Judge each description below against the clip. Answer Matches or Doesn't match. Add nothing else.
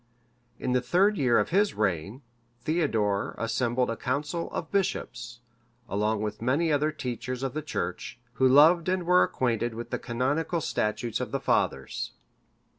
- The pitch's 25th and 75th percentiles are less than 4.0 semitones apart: Doesn't match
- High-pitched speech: Doesn't match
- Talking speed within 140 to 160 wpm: Matches